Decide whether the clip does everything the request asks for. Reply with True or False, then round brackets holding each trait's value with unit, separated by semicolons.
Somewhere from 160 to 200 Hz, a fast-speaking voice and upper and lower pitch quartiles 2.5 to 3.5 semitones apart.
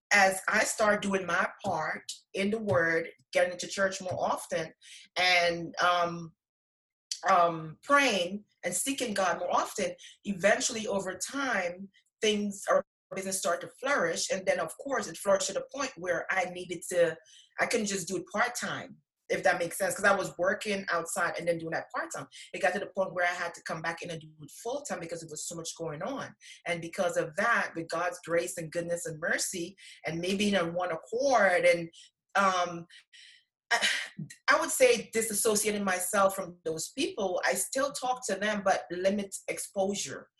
False (185 Hz; 185 wpm; 3.2 semitones)